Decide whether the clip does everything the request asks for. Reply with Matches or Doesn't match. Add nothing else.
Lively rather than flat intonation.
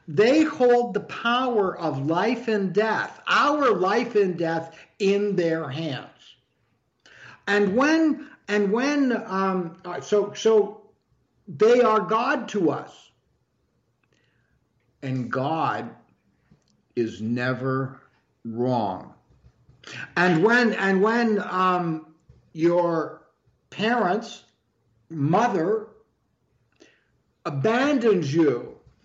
Matches